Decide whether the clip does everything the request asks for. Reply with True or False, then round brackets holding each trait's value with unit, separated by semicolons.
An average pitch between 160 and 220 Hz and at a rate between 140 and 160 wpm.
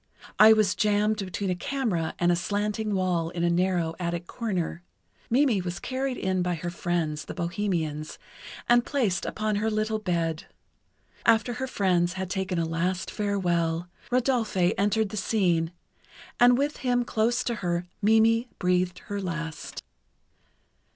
True (190 Hz; 150 wpm)